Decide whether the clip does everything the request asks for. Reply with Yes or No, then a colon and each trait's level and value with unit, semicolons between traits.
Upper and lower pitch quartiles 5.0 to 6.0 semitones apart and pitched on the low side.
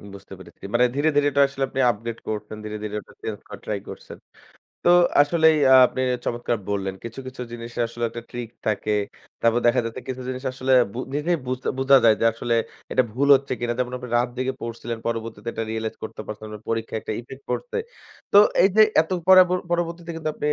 No: average, 3.4 semitones; low, 120 Hz